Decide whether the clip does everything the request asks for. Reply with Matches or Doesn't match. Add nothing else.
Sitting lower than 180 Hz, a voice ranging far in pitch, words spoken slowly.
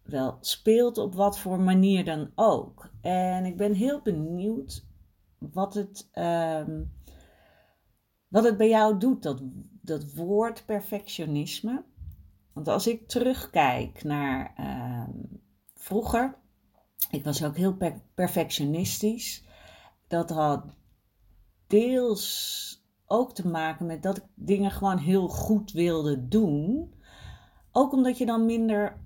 Doesn't match